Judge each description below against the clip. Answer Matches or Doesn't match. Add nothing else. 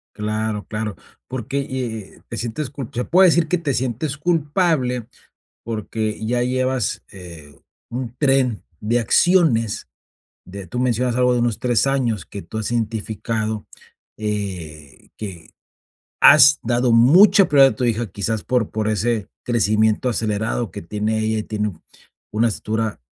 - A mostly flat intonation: Doesn't match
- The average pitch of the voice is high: Doesn't match